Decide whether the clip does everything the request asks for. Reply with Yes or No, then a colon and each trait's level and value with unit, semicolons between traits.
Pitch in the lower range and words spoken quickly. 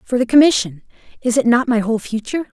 No: high, 240 Hz; fast, 210 wpm